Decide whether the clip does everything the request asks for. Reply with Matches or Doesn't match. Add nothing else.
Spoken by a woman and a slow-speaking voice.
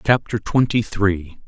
Doesn't match